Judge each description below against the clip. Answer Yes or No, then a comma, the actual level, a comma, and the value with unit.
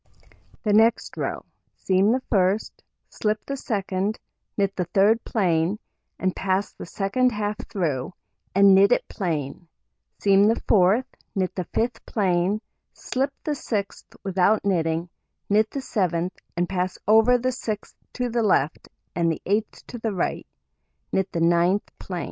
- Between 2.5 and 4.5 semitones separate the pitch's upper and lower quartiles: Yes, average, 3.3 semitones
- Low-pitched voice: No, high, 200 Hz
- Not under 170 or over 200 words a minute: No, average, 150 wpm